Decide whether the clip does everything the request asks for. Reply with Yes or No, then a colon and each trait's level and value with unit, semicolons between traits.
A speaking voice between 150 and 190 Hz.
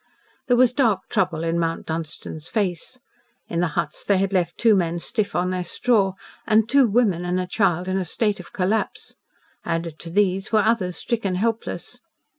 Yes: medium, 185 Hz